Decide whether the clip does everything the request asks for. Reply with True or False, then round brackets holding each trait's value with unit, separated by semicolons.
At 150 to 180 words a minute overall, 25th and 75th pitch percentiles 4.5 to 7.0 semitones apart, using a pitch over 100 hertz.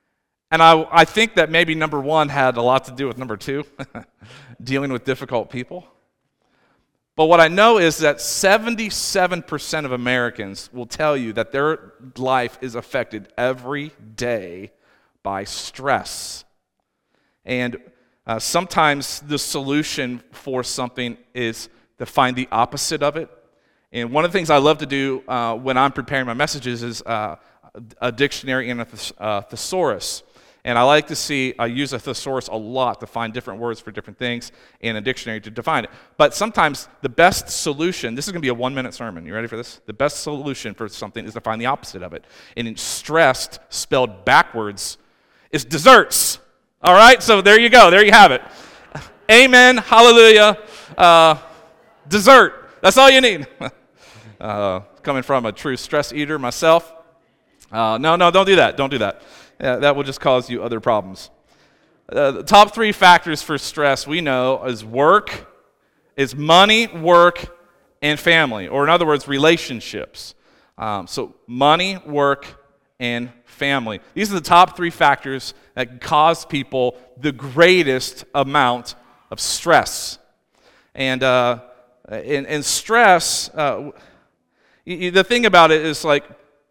True (165 wpm; 4.9 semitones; 140 Hz)